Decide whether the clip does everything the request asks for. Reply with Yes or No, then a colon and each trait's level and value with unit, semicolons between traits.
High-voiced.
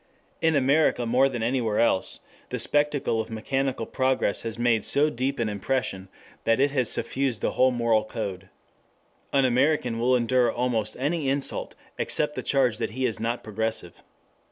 No: low, 125 Hz